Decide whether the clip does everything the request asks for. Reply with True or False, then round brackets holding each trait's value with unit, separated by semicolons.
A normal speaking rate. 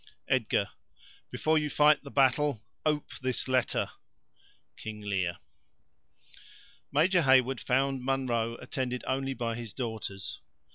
False (100 wpm)